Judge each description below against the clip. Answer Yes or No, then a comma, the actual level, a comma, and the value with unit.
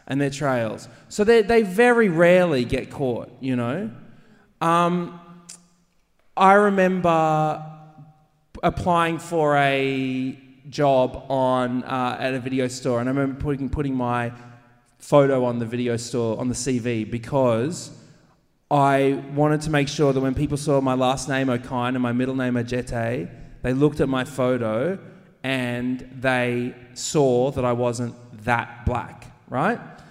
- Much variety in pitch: No, average, 3.7 semitones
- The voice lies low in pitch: Yes, low, 130 Hz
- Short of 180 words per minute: Yes, average, 145 wpm